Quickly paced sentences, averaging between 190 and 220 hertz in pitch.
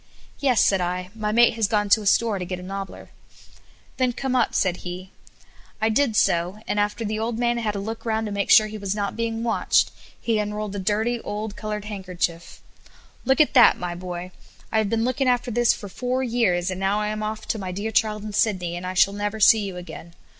Yes: fast, 230 wpm; high, 210 Hz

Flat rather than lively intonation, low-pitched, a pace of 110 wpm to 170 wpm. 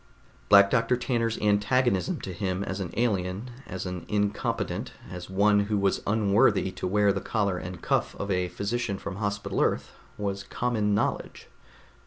Yes: narrow, 2.0 semitones; low, 100 Hz; average, 160 wpm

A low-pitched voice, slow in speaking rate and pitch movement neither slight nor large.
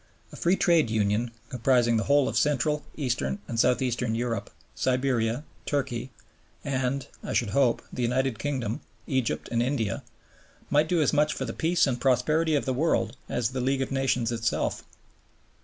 No: low, 130 Hz; average, 170 wpm; average, 3.3 semitones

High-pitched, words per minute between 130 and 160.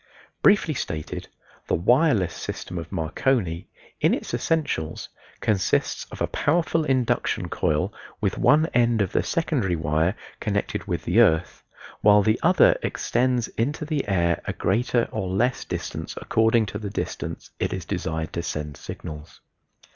No: low, 105 Hz; average, 145 wpm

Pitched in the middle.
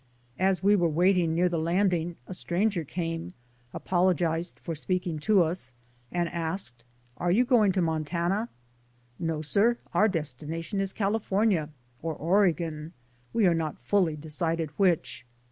Yes: medium, 175 Hz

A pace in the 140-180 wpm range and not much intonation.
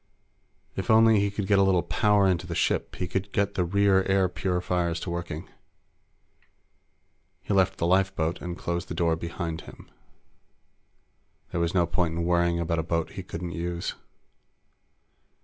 Yes: average, 165 wpm; narrow, 2.2 semitones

